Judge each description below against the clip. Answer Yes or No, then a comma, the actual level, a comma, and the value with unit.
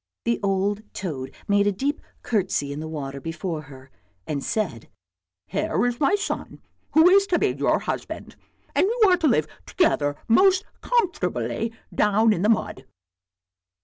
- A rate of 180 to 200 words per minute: No, average, 160 wpm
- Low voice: No, high, 200 Hz